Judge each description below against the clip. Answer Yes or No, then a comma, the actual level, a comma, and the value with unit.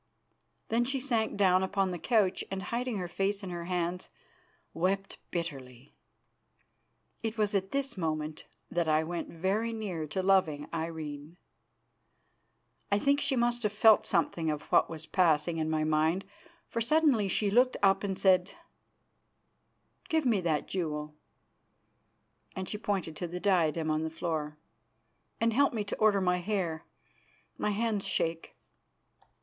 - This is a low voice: No, medium, 185 Hz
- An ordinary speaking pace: Yes, average, 150 wpm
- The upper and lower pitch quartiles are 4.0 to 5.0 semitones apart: Yes, average, 4.7 semitones